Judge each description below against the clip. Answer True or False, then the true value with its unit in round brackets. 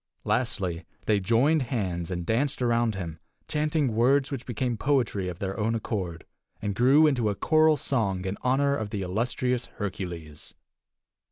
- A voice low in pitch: True (115 Hz)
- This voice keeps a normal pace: True (155 wpm)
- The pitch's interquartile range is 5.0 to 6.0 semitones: True (5.5 semitones)